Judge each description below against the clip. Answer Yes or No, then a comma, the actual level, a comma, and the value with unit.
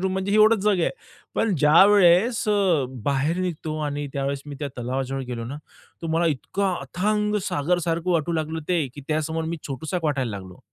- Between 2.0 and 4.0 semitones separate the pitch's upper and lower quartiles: No, average, 4.7 semitones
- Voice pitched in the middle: Yes, medium, 160 Hz